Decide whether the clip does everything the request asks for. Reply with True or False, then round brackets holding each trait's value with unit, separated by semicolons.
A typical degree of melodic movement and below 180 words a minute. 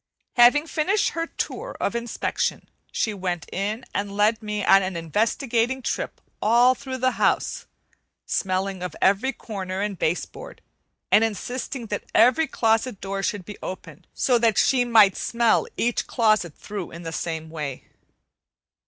True (4.2 semitones; 155 wpm)